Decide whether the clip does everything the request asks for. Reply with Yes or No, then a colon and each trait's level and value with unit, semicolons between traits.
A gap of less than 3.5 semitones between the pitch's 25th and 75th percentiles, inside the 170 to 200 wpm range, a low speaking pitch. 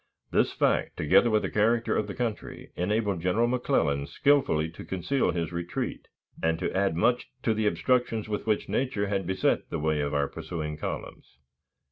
No: wide, 5.6 semitones; average, 175 wpm; low, 100 Hz